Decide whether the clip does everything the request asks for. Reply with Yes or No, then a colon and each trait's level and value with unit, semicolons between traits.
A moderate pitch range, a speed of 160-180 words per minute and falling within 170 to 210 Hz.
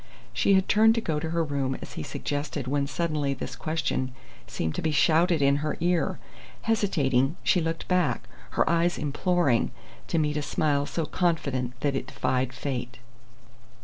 No: average, 3.8 semitones; average, 170 wpm; medium, 150 Hz